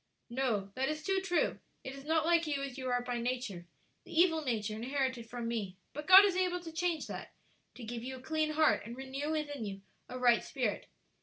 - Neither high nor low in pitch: No, very high, 265 Hz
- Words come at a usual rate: No, fast, 220 wpm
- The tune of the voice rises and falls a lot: No, average, 4.8 semitones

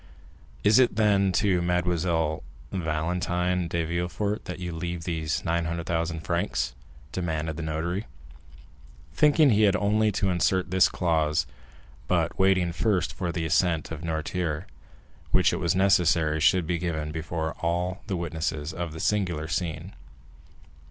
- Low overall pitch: Yes, very low, 85 Hz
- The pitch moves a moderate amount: No, narrow, 2.3 semitones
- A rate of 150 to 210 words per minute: No, average, 140 wpm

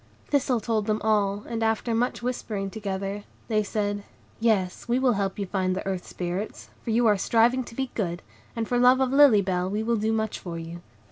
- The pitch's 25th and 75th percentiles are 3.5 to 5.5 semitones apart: No, average, 3.1 semitones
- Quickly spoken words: Yes, fast, 215 wpm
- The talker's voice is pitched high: Yes, high, 215 Hz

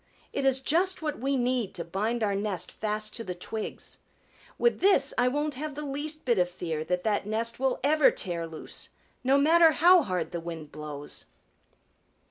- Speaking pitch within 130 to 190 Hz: No, high, 230 Hz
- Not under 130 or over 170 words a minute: No, average, 185 wpm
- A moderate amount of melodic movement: No, wide, 8.3 semitones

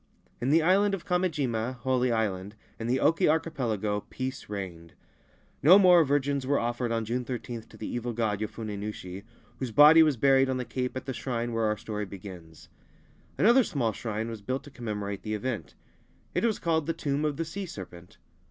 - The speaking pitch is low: Yes, low, 120 Hz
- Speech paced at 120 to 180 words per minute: No, average, 190 wpm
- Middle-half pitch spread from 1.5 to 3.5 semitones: No, average, 5.2 semitones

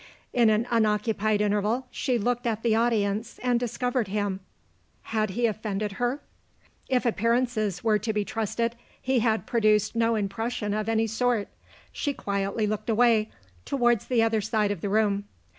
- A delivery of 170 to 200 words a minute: No, average, 160 wpm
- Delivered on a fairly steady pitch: Yes, narrow, 2.2 semitones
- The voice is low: No, high, 220 Hz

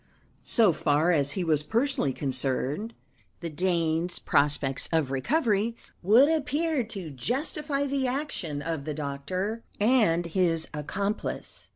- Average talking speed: No, slow, 120 wpm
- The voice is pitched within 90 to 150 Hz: No, medium, 180 Hz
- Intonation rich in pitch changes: Yes, wide, 8.0 semitones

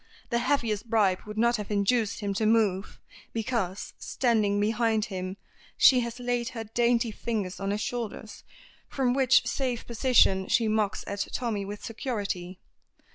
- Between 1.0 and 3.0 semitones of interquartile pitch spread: Yes, average, 2.7 semitones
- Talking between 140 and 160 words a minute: Yes, average, 150 wpm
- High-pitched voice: Yes, high, 220 Hz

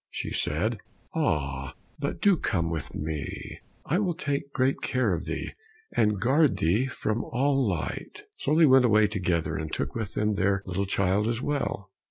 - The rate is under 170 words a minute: No, average, 175 wpm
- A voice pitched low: Yes, low, 105 Hz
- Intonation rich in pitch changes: Yes, wide, 6.8 semitones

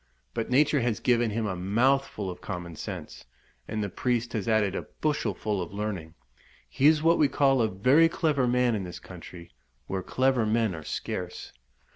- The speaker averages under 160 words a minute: No, average, 180 wpm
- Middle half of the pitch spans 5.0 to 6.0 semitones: Yes, average, 5.3 semitones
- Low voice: Yes, low, 110 Hz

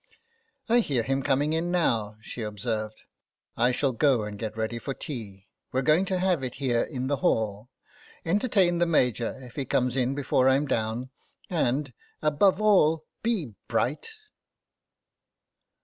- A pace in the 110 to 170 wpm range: Yes, average, 160 wpm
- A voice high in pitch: No, low, 130 Hz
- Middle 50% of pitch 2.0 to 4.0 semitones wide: No, wide, 5.5 semitones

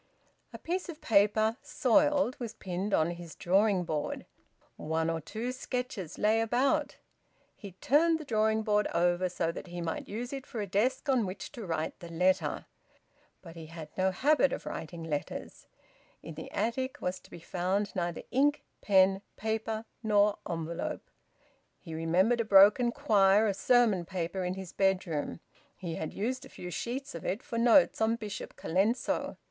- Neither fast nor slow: Yes, average, 170 wpm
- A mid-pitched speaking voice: No, high, 200 Hz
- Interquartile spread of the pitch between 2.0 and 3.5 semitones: No, average, 5.3 semitones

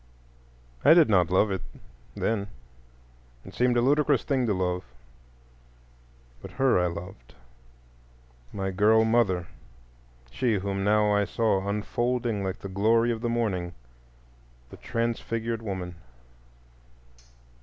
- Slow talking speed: Yes, slow, 115 wpm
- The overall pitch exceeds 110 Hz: No, low, 105 Hz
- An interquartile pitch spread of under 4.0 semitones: No, average, 4.3 semitones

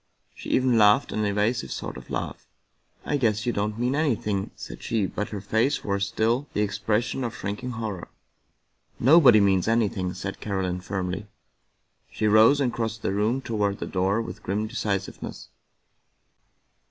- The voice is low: Yes, low, 105 Hz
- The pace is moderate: Yes, average, 165 wpm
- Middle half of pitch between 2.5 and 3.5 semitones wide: Yes, average, 2.8 semitones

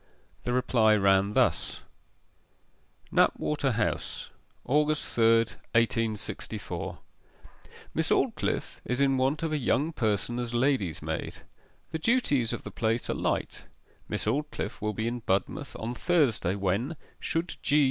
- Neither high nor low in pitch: No, low, 120 Hz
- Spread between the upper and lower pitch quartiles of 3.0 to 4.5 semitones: No, average, 4.9 semitones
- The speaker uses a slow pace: Yes, slow, 130 wpm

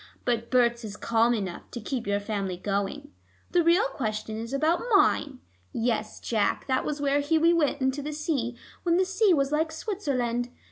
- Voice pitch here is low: No, very high, 260 Hz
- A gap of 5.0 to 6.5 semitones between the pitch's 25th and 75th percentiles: Yes, average, 5.3 semitones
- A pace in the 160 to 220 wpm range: Yes, average, 180 wpm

